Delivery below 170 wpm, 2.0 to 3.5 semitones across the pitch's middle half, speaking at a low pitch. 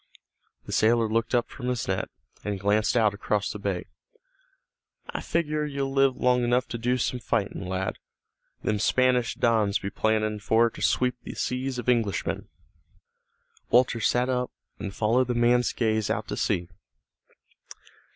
Yes: average, 155 wpm; average, 3.0 semitones; low, 115 Hz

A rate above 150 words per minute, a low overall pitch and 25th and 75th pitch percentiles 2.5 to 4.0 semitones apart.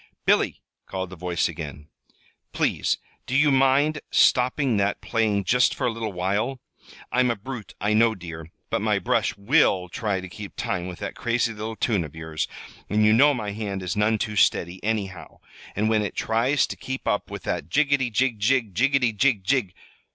No: average, 190 wpm; low, 110 Hz; average, 4.7 semitones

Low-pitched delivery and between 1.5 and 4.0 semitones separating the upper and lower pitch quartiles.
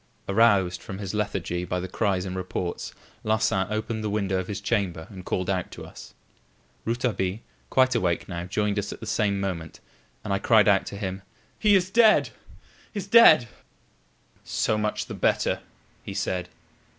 Yes: low, 100 Hz; average, 2.9 semitones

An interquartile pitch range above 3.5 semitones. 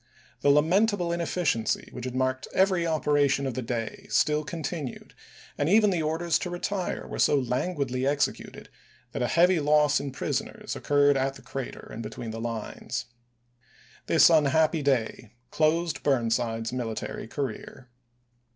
Yes: average, 4.9 semitones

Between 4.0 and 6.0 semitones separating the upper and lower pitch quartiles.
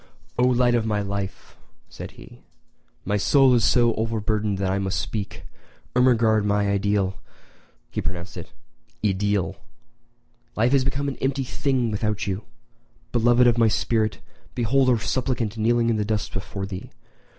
No: average, 3.2 semitones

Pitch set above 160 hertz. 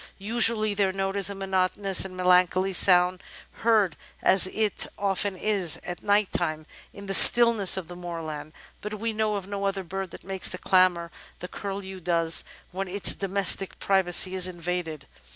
Yes: high, 190 Hz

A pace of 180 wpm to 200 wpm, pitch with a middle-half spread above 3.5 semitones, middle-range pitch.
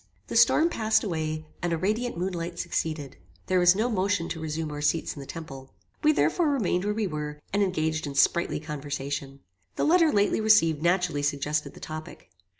Yes: average, 190 wpm; average, 5.2 semitones; medium, 165 Hz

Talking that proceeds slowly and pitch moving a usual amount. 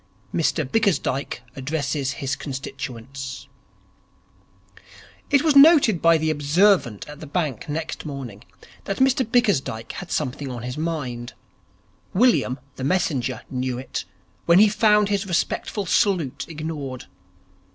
No: slow, 125 wpm; wide, 6.8 semitones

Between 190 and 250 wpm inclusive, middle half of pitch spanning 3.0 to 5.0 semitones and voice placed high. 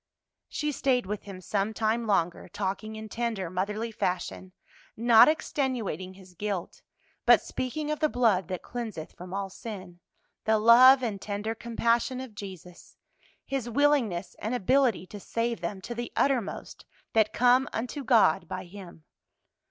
No: average, 150 wpm; average, 4.3 semitones; high, 220 Hz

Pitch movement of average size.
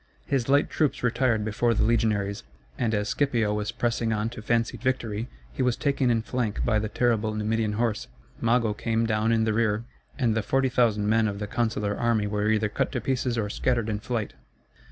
No: narrow, 2.1 semitones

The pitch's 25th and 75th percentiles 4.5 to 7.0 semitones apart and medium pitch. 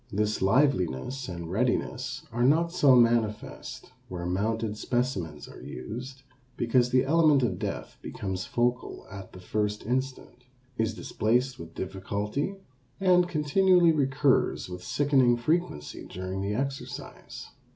No: wide, 5.6 semitones; low, 120 Hz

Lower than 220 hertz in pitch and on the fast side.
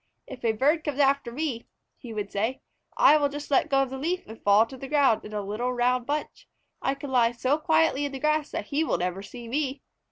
No: very high, 265 Hz; fast, 245 wpm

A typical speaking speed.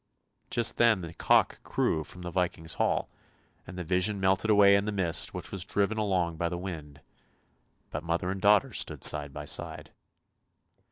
Yes: average, 175 wpm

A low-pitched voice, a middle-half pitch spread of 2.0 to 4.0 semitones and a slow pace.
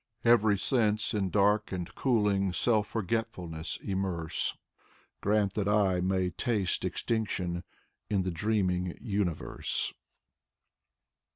Yes: low, 100 Hz; average, 2.8 semitones; slow, 105 wpm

